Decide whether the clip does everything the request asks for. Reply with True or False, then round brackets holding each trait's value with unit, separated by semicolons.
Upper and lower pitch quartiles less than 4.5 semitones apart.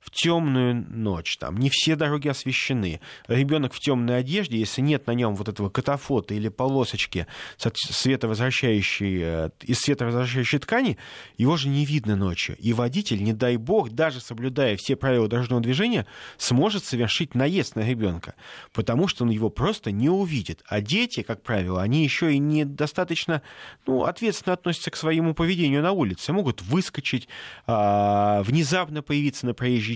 False (5.1 semitones)